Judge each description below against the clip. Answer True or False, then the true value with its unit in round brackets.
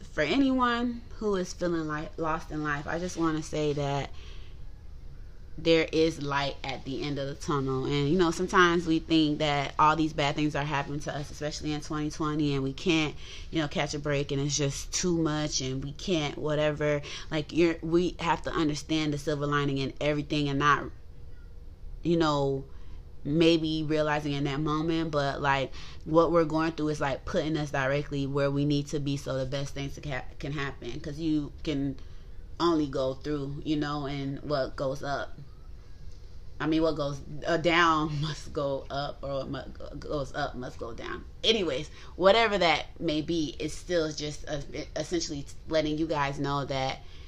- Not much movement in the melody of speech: True (2.2 semitones)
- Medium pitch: True (150 Hz)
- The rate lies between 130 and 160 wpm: False (180 wpm)